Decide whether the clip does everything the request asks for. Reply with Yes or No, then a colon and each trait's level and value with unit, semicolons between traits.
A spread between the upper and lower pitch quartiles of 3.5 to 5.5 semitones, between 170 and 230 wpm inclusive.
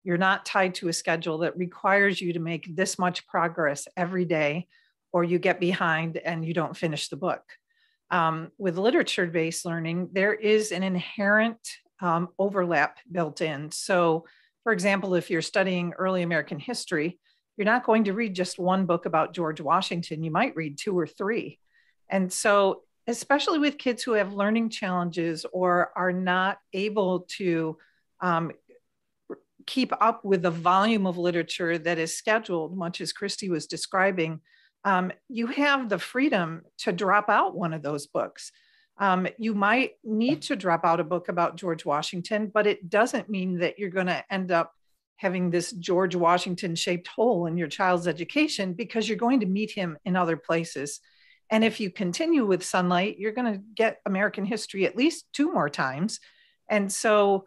Yes: average, 3.8 semitones; average, 175 wpm